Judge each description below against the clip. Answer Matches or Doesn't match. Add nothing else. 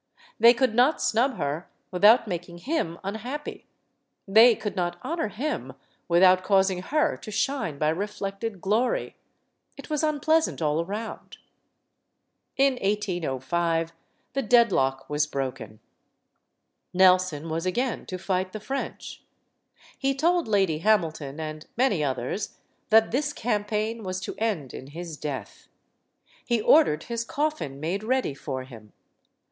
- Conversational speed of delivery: Doesn't match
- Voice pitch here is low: Doesn't match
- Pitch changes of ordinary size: Doesn't match